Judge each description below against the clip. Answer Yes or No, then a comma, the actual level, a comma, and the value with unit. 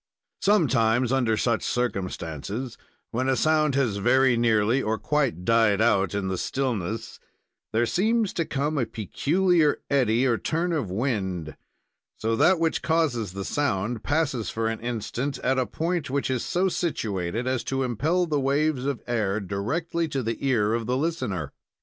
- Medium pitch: No, low, 125 Hz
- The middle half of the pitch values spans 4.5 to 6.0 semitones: Yes, average, 5.1 semitones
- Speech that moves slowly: No, average, 160 wpm